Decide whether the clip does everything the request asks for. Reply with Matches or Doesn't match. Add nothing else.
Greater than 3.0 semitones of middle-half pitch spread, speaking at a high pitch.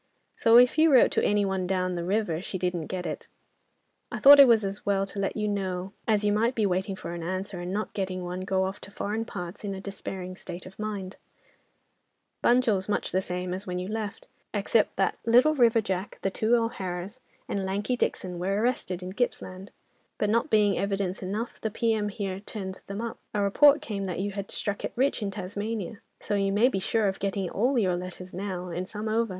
Doesn't match